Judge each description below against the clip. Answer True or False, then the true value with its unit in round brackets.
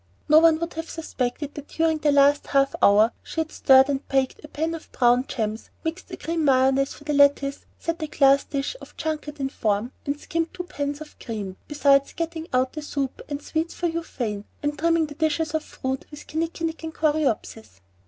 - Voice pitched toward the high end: True (290 Hz)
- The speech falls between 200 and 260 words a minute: True (205 wpm)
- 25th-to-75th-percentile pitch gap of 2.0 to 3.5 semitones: True (3.1 semitones)